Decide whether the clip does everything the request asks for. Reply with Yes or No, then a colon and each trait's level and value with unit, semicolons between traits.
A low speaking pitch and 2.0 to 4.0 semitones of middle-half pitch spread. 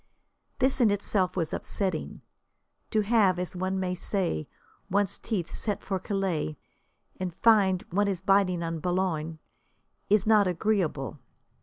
No: high, 190 Hz; narrow, 2.5 semitones